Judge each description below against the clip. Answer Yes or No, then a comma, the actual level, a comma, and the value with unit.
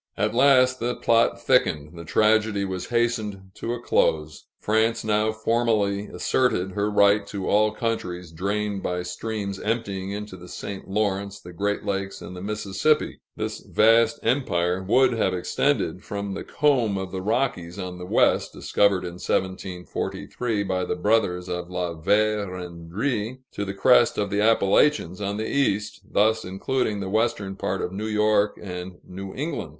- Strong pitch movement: No, average, 3.0 semitones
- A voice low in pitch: Yes, low, 100 Hz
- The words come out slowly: No, average, 155 wpm